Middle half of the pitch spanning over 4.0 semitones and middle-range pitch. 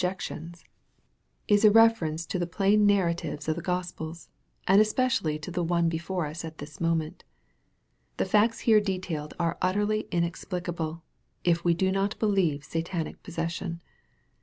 No: average, 3.1 semitones; medium, 175 Hz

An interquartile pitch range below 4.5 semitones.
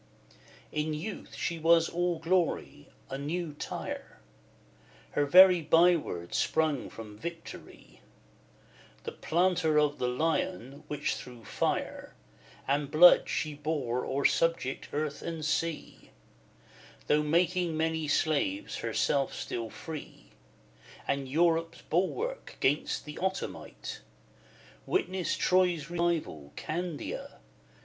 Yes: average, 3.1 semitones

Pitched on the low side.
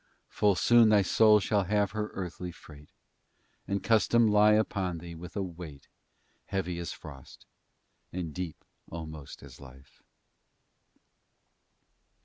Yes: very low, 90 Hz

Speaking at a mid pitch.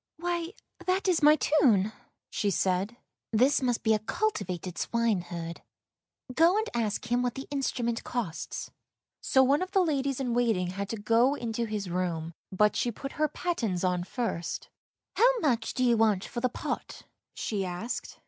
No: high, 235 Hz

